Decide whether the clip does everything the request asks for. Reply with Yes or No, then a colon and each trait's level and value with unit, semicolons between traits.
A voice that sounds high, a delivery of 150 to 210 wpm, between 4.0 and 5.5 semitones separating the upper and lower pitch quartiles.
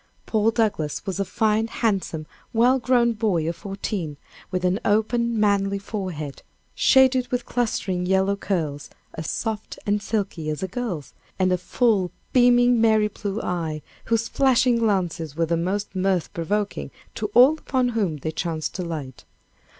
Yes: high, 200 Hz; average, 155 wpm; average, 4.7 semitones